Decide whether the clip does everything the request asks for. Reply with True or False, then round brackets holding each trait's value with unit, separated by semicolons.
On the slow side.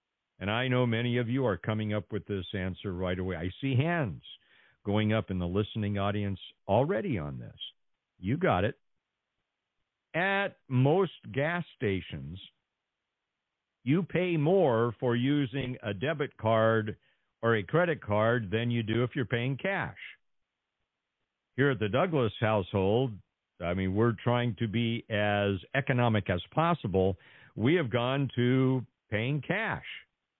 False (145 wpm)